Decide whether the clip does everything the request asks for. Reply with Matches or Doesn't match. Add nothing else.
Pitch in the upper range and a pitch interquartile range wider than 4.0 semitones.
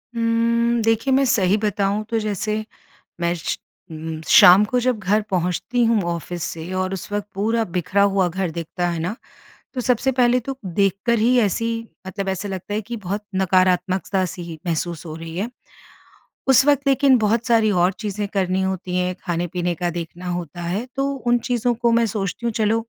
Matches